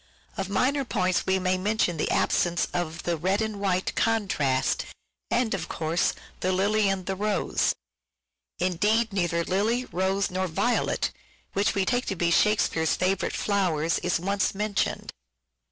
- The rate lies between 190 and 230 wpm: No, average, 160 wpm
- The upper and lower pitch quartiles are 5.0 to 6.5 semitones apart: No, average, 3.0 semitones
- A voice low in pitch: No, high, 190 Hz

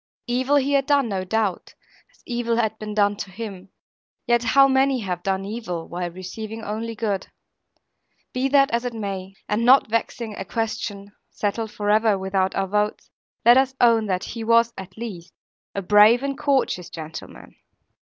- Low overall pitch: No, high, 220 Hz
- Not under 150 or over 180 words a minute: Yes, average, 170 wpm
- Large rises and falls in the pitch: No, average, 3.5 semitones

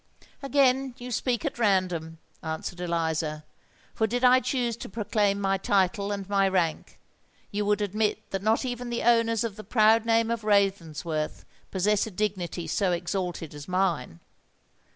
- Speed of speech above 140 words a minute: Yes, average, 155 wpm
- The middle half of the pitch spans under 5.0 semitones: Yes, average, 4.3 semitones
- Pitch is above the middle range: Yes, high, 200 Hz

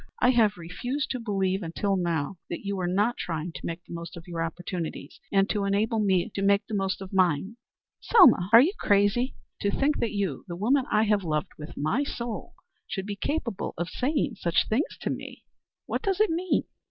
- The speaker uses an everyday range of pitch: Yes, average, 4.9 semitones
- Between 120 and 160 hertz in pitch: No, high, 200 Hz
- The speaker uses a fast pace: Yes, fast, 210 wpm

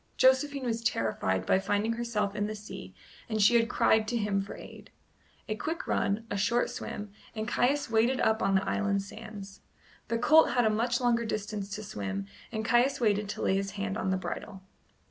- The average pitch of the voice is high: Yes, high, 215 Hz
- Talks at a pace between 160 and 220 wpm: Yes, average, 200 wpm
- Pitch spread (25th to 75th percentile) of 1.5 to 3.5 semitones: Yes, average, 2.8 semitones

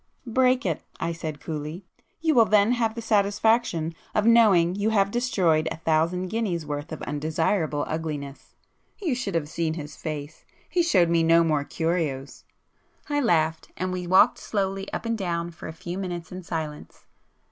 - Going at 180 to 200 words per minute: No, average, 165 wpm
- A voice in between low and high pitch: Yes, medium, 175 Hz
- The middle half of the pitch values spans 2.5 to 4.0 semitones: No, average, 4.9 semitones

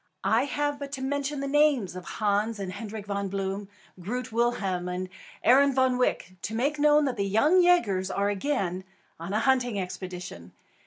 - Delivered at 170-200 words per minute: Yes, average, 175 wpm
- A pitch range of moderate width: No, wide, 6.3 semitones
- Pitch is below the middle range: No, high, 220 Hz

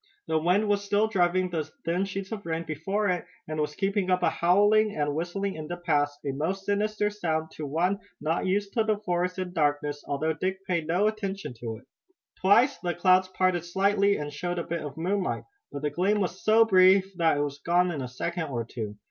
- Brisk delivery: Yes, fast, 215 wpm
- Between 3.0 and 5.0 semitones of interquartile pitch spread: Yes, average, 4.0 semitones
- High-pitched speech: No, medium, 180 Hz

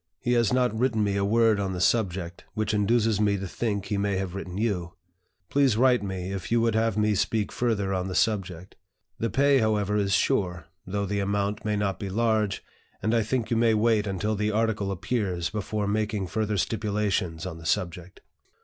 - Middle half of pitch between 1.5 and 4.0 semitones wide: Yes, narrow, 2.5 semitones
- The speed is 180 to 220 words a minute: Yes, average, 200 wpm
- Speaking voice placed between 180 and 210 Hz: No, low, 105 Hz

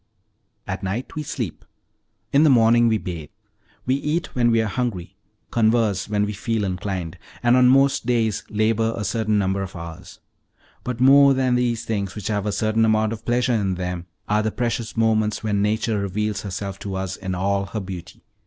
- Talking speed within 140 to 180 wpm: No, average, 190 wpm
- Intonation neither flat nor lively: Yes, average, 3.2 semitones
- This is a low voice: Yes, low, 110 Hz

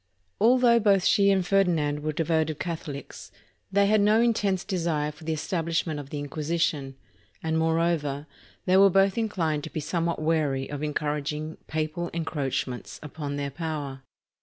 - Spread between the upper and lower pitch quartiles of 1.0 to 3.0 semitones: No, average, 3.8 semitones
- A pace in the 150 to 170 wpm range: Yes, average, 155 wpm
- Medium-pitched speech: Yes, medium, 160 Hz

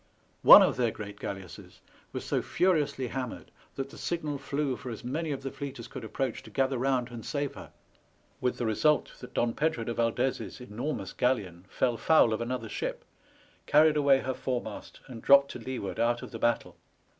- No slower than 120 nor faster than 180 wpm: No, average, 195 wpm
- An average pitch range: Yes, average, 3.3 semitones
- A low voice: Yes, low, 125 Hz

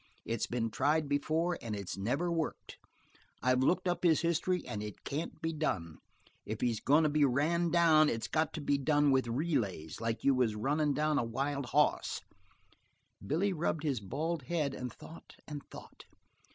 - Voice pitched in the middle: Yes, medium, 145 Hz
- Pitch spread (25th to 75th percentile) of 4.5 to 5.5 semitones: Yes, average, 4.9 semitones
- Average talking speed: Yes, average, 180 wpm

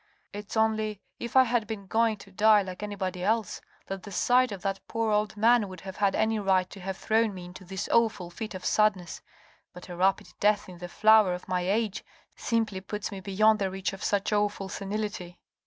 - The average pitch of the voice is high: Yes, high, 205 Hz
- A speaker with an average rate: No, fast, 215 wpm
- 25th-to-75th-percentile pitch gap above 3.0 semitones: No, narrow, 2.5 semitones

